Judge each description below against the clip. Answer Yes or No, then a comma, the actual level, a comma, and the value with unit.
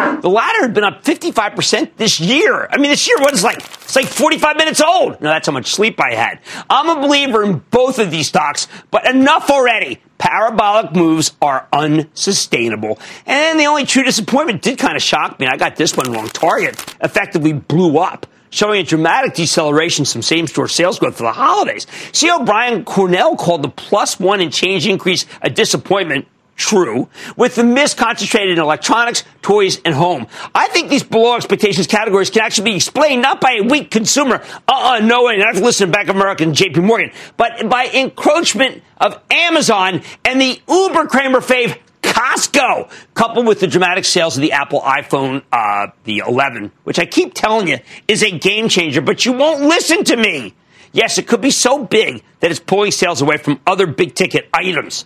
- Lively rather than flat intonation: Yes, wide, 7.1 semitones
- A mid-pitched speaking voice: No, high, 210 Hz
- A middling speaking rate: Yes, average, 195 wpm